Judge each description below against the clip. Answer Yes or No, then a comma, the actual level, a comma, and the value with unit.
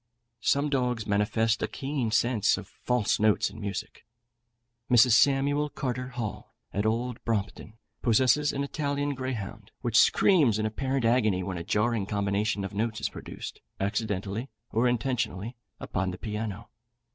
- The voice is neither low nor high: No, low, 115 Hz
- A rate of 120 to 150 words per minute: Yes, average, 145 wpm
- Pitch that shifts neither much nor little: Yes, average, 3.7 semitones